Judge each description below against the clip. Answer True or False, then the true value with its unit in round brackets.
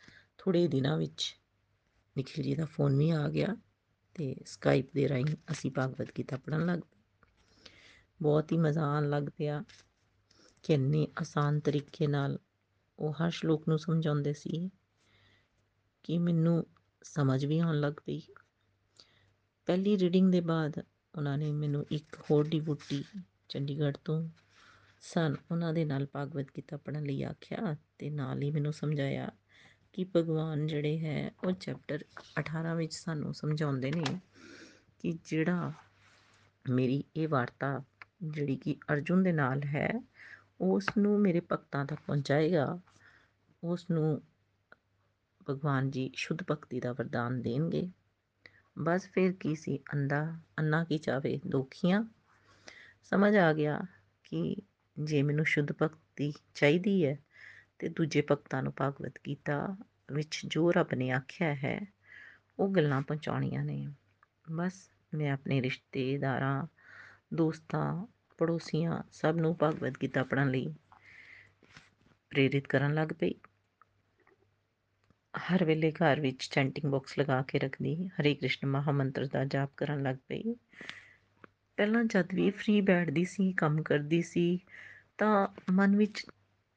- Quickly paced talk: False (130 wpm)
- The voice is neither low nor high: True (150 Hz)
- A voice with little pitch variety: False (3.6 semitones)